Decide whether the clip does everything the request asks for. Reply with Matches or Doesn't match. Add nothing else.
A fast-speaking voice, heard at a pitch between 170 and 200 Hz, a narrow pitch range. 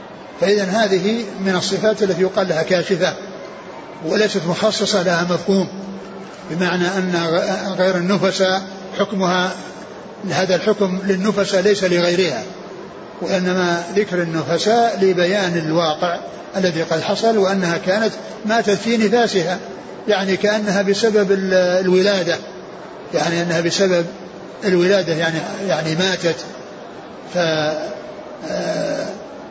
Doesn't match